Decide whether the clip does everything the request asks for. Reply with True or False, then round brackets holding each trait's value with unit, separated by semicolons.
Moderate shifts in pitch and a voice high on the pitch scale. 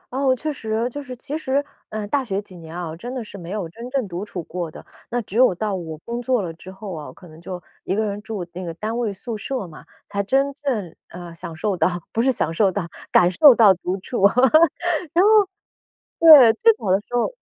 False (6.0 semitones; 215 Hz)